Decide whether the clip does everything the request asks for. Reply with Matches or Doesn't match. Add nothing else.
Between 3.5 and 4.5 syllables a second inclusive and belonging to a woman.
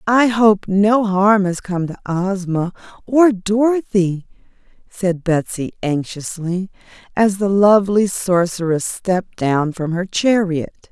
Matches